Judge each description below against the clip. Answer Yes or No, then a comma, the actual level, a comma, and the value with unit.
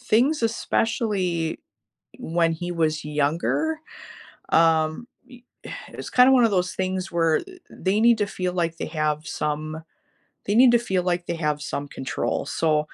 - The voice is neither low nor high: Yes, medium, 175 Hz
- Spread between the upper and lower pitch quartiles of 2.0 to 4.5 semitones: No, wide, 5.6 semitones